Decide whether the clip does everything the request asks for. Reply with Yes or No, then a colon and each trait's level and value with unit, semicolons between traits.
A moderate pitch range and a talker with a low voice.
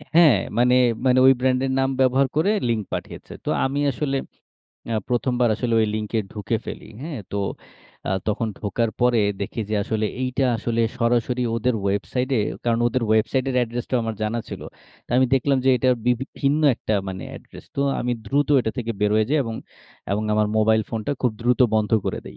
Yes: average, 3.0 semitones; low, 120 Hz